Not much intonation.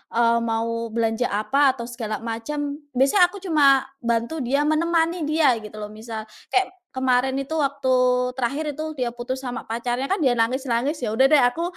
No: average, 4.3 semitones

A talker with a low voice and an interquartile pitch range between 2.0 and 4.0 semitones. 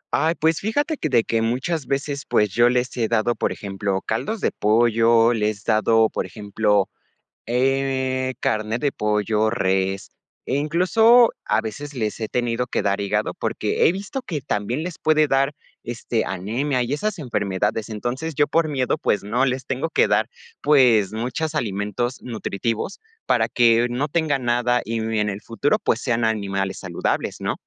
No: low, 120 Hz; average, 4.8 semitones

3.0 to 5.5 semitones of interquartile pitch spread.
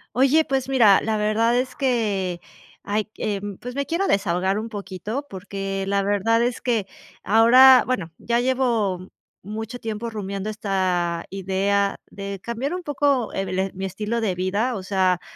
Yes: average, 4.0 semitones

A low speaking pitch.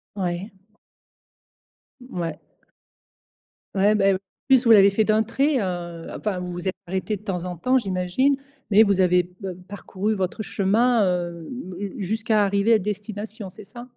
No: high, 200 Hz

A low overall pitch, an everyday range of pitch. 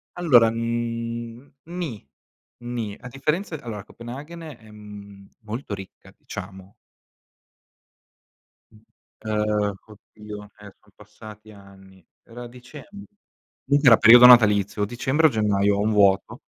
Yes: low, 110 Hz; average, 3.1 semitones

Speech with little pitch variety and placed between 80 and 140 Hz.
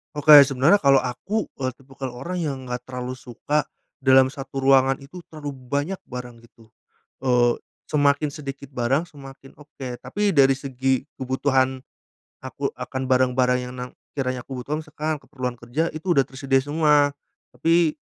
Yes: narrow, 2.3 semitones; low, 135 Hz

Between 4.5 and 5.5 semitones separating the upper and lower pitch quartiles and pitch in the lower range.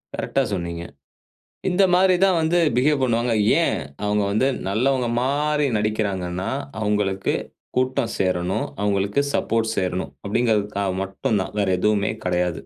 Yes: average, 5.0 semitones; low, 105 Hz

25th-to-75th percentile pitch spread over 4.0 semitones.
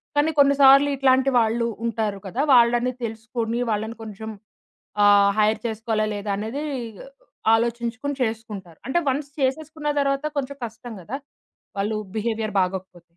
No: average, 3.7 semitones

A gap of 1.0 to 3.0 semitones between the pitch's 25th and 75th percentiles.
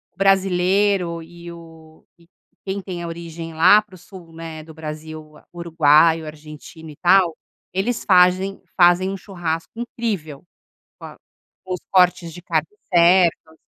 Yes: narrow, 2.6 semitones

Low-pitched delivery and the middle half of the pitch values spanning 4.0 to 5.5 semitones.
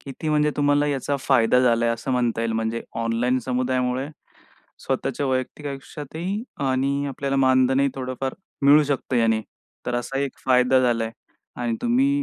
No: low, 130 Hz; narrow, 2.4 semitones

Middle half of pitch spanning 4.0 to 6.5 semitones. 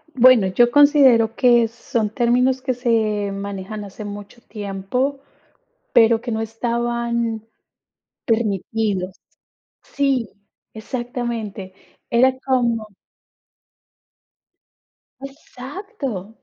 No: average, 3.0 semitones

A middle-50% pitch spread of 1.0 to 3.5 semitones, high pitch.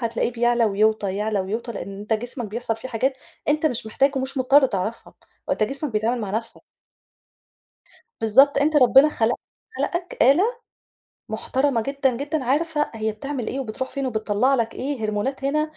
No: average, 4.0 semitones; high, 245 Hz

